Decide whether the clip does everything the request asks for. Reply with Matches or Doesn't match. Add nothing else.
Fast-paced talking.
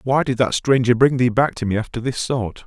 Matches